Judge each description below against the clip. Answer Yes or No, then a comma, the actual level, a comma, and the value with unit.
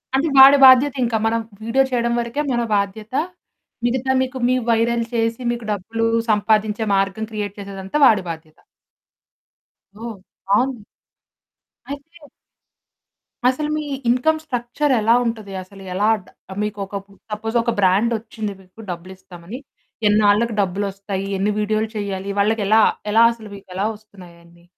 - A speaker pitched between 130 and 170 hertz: No, high, 220 Hz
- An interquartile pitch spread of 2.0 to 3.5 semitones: Yes, average, 3.1 semitones